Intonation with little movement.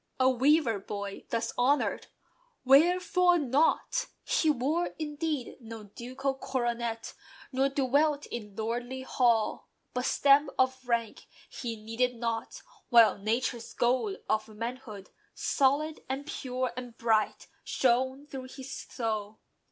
No: average, 3.3 semitones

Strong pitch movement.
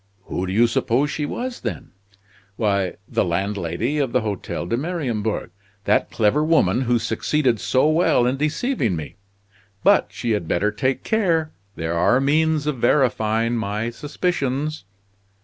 Yes: wide, 6.1 semitones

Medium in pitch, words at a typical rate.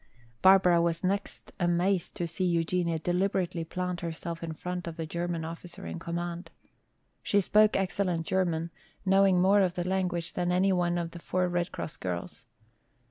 Yes: medium, 175 Hz; average, 165 wpm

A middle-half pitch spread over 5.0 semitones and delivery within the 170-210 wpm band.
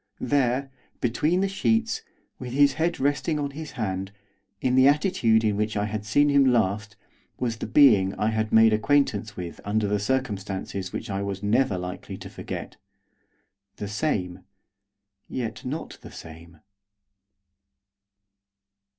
No: wide, 5.6 semitones; average, 140 wpm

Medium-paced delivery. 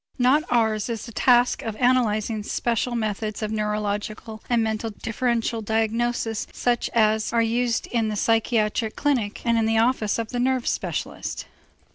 Yes: average, 155 wpm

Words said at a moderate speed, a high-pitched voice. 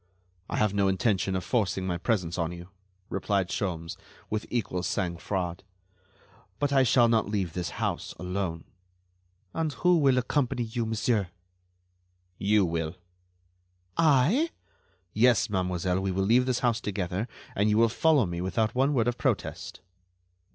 No: average, 150 wpm; low, 105 Hz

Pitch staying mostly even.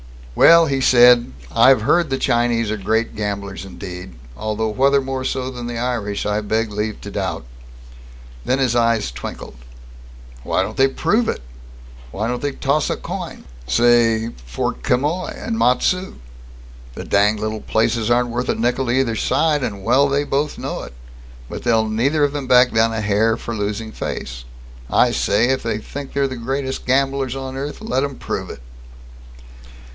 No: average, 3.7 semitones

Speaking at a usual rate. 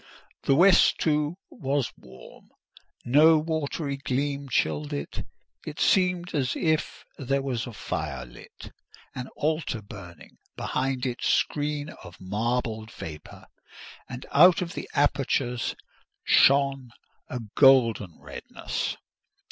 No: slow, 110 wpm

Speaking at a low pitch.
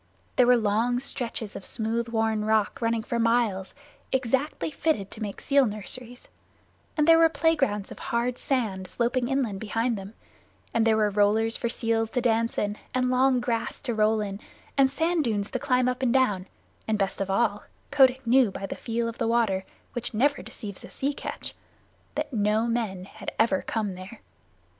No: high, 230 Hz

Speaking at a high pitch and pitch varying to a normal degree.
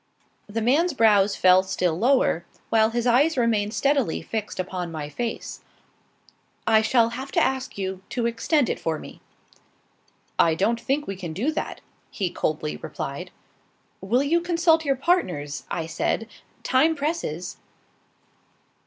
No: high, 225 Hz; wide, 6.8 semitones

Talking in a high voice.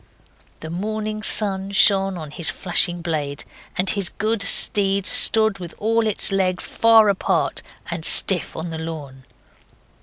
Yes: high, 195 Hz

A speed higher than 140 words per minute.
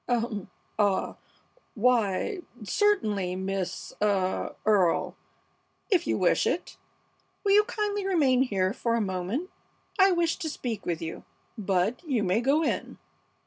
No: slow, 135 wpm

